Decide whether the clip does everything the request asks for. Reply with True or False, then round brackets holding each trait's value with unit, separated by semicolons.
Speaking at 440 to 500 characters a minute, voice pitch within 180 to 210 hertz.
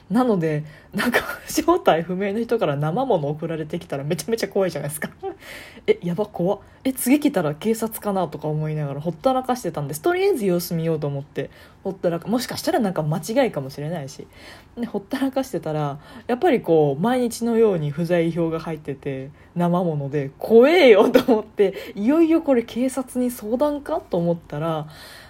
False (390 characters per minute; 190 Hz)